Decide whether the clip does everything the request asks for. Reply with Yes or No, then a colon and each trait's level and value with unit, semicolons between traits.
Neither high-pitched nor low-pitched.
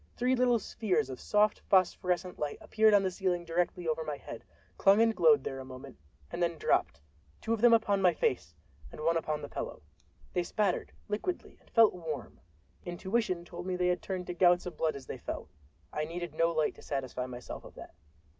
Yes: medium, 175 Hz